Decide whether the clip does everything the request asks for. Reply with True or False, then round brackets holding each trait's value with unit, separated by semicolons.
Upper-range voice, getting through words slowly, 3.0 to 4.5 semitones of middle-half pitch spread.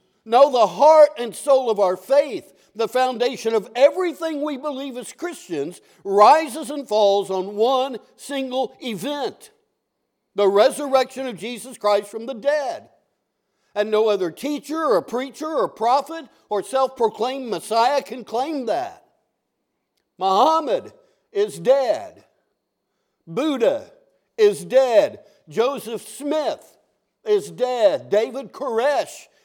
False (260 Hz; 115 wpm; 5.1 semitones)